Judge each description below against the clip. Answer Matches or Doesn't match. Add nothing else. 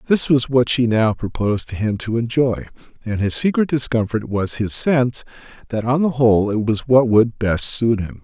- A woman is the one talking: Doesn't match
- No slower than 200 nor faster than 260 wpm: Matches